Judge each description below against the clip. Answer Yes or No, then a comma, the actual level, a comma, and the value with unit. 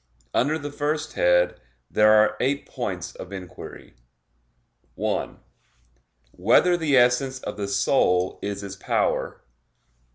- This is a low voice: Yes, low, 110 Hz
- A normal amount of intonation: No, wide, 6.3 semitones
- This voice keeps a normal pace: No, slow, 120 wpm